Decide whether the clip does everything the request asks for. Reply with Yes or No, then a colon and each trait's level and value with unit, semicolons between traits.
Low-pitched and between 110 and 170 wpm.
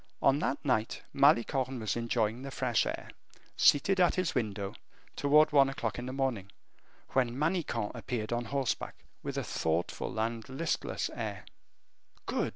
Yes: low, 125 Hz; average, 150 wpm